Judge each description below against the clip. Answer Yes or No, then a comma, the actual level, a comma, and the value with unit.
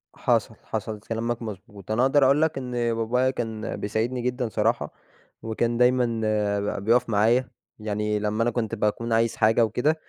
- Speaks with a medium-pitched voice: No, low, 115 Hz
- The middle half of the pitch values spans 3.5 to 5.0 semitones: No, narrow, 2.5 semitones